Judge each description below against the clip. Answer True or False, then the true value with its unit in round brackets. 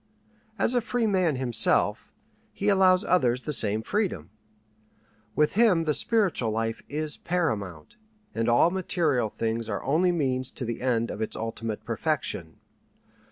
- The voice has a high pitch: False (135 Hz)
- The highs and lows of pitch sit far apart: True (8.1 semitones)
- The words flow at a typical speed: True (145 wpm)